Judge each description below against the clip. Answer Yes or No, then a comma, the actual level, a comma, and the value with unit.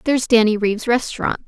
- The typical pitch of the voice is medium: No, high, 230 Hz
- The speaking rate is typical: Yes, average, 165 wpm